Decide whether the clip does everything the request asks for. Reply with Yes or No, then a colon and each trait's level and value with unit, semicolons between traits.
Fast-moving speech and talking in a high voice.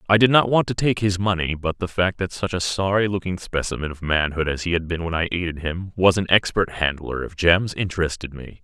No: fast, 245 wpm; very low, 90 Hz